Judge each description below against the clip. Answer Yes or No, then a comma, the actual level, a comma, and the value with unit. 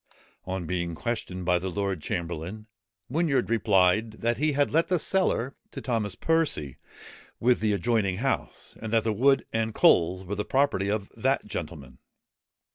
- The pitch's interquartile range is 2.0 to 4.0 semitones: No, average, 5.2 semitones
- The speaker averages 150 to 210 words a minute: Yes, average, 160 wpm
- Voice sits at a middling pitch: No, low, 105 Hz